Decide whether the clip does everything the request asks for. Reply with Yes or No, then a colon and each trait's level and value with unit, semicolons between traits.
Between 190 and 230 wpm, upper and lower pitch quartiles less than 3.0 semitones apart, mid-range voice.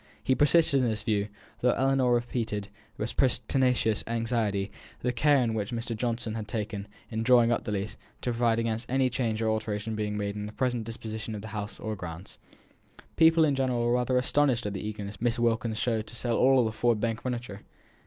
No: average, 200 wpm; narrow, 2.6 semitones; low, 115 Hz